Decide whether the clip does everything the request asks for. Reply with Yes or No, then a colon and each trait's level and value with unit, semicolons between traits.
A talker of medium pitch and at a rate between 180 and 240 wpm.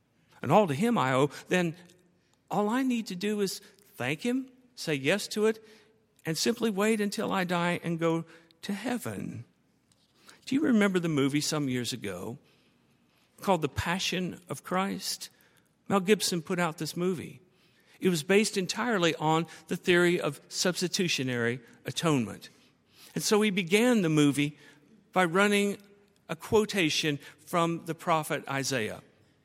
No: medium, 180 Hz; average, 145 wpm